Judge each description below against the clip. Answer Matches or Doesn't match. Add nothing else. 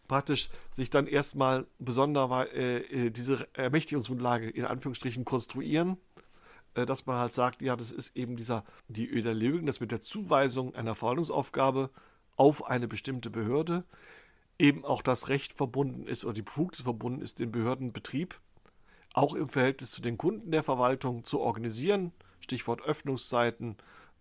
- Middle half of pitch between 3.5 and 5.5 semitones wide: Doesn't match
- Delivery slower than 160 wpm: Matches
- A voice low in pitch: Matches